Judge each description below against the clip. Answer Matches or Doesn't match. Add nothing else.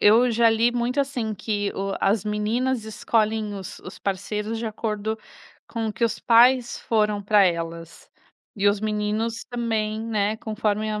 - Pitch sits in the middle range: Doesn't match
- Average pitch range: Doesn't match